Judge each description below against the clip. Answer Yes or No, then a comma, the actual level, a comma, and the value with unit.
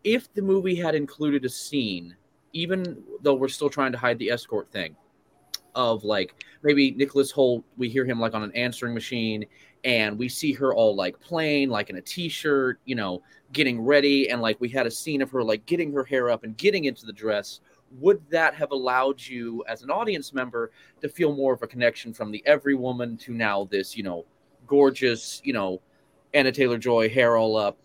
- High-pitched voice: No, low, 130 Hz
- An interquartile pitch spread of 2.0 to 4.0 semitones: Yes, average, 3.7 semitones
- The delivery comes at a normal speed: No, fast, 210 wpm